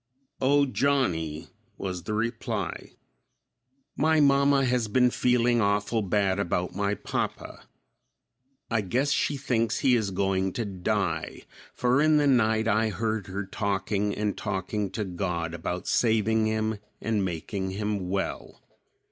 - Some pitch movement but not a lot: Yes, average, 3.9 semitones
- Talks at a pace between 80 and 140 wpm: Yes, slow, 135 wpm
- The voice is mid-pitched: No, low, 105 Hz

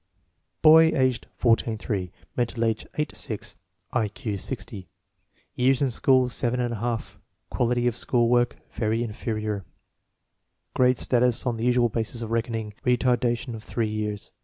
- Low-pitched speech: Yes, low, 120 Hz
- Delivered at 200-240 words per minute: No, average, 150 wpm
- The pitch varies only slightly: Yes, narrow, 2.1 semitones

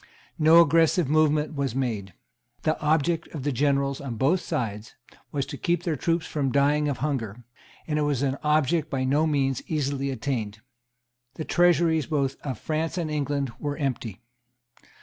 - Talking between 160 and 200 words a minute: Yes, average, 165 wpm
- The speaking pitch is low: No, medium, 145 Hz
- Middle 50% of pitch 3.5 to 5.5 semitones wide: No, average, 2.8 semitones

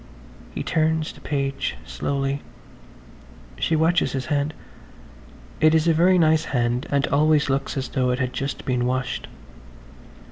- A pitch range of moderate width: Yes, average, 3.3 semitones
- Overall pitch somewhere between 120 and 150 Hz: Yes, medium, 140 Hz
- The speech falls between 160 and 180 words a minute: No, average, 140 wpm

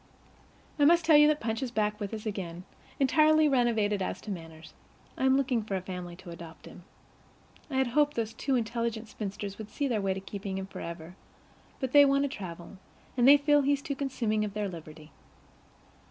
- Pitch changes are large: Yes, wide, 6.1 semitones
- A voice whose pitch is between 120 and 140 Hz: No, high, 220 Hz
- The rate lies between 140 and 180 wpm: No, average, 200 wpm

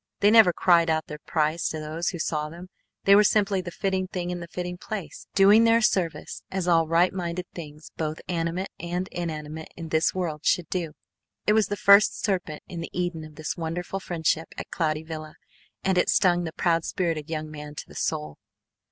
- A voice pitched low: No, medium, 170 Hz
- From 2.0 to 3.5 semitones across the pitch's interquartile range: Yes, average, 2.7 semitones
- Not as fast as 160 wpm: No, fast, 205 wpm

